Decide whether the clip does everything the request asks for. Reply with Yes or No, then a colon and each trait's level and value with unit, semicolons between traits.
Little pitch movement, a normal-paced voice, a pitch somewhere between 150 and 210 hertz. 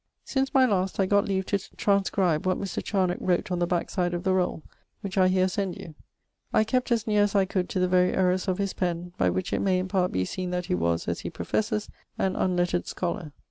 No: narrow, 2.0 semitones; fast, 240 wpm; medium, 185 Hz